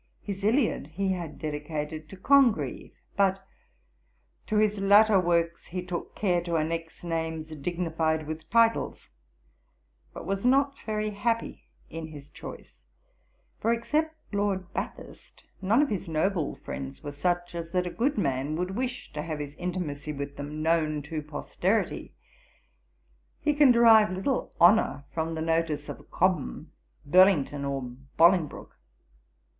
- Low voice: No, medium, 175 Hz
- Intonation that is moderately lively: Yes, average, 4.7 semitones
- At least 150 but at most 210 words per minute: No, average, 140 wpm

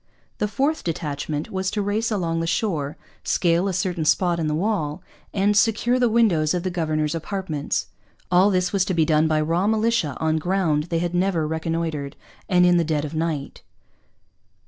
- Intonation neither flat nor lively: Yes, average, 3.8 semitones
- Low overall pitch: No, medium, 170 Hz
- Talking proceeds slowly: No, average, 185 wpm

